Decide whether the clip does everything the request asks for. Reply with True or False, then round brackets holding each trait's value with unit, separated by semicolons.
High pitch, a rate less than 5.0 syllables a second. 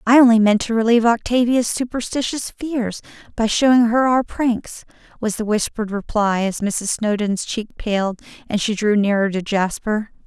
True (220 Hz; 4.8 syllables/s)